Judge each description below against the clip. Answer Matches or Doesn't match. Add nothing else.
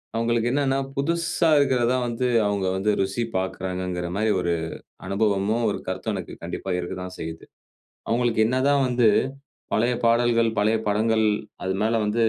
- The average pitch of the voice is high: Doesn't match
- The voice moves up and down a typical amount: Matches